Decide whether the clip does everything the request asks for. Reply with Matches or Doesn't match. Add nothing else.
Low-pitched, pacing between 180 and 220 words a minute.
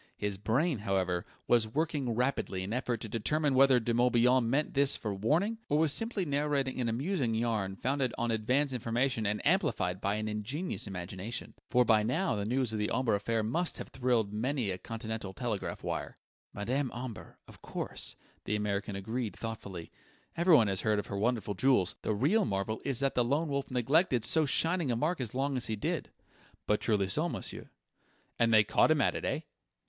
Matches